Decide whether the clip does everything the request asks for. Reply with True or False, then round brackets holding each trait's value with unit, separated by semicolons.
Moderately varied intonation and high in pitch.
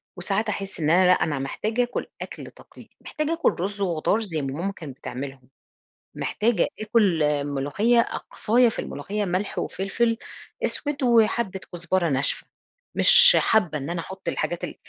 False (5.9 semitones; 195 Hz)